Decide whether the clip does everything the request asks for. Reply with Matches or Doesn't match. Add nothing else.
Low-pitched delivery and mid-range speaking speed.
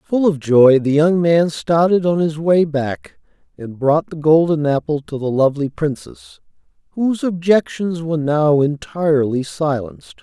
Doesn't match